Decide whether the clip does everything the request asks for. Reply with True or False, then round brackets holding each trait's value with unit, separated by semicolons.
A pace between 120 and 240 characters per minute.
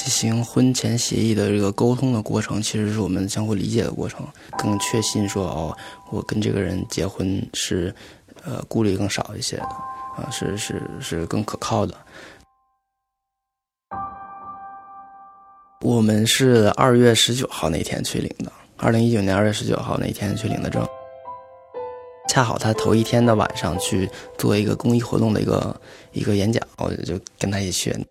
False (250 characters per minute)